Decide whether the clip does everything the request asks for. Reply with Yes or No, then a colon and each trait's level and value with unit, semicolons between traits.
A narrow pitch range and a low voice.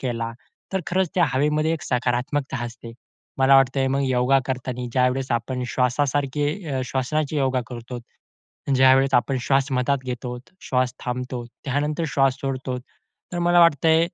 Yes: narrow, 2.3 semitones; low, 130 Hz